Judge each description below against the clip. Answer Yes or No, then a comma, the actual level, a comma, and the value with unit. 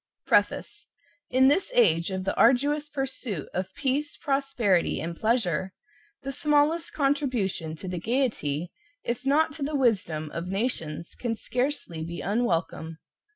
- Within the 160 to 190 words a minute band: No, slow, 135 wpm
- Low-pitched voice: No, high, 235 Hz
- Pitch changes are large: Yes, wide, 7.8 semitones